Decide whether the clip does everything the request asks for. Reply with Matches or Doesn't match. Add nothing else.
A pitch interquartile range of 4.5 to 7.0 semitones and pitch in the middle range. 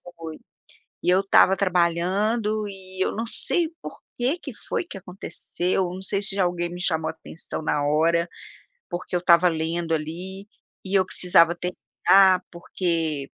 Doesn't match